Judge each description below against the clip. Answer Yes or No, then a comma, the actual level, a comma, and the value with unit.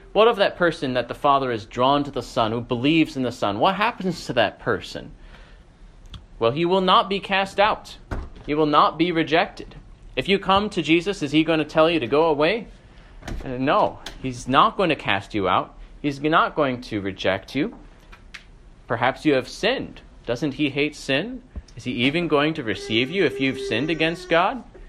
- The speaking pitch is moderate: Yes, medium, 150 Hz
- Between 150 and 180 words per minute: No, average, 200 wpm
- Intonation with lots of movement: Yes, wide, 5.8 semitones